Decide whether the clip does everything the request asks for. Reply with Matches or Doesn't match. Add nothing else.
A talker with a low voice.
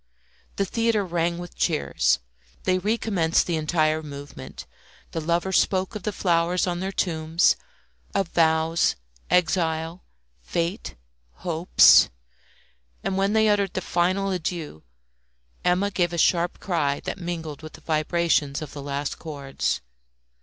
Doesn't match